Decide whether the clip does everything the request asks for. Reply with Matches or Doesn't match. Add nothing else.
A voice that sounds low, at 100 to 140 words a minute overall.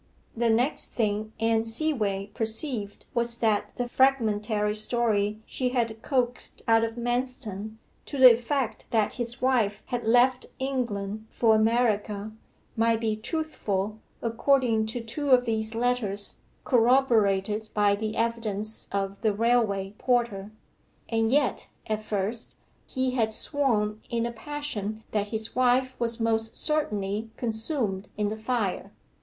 Doesn't match